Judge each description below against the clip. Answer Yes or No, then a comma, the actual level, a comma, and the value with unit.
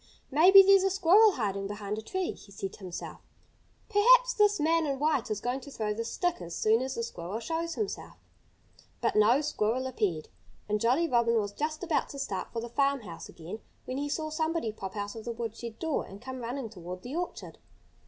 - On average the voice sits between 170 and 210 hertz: No, high, 245 Hz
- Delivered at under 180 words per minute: No, fast, 205 wpm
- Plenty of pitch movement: Yes, wide, 7.2 semitones